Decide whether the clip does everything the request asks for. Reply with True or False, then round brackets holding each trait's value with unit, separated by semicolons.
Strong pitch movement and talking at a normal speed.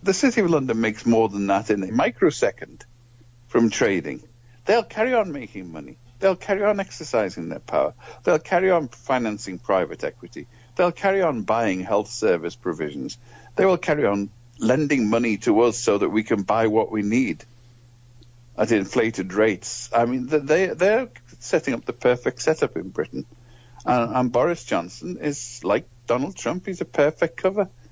True (5.8 semitones; 165 wpm)